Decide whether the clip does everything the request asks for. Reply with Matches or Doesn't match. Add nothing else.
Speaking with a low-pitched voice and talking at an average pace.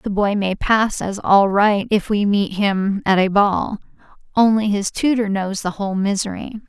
Doesn't match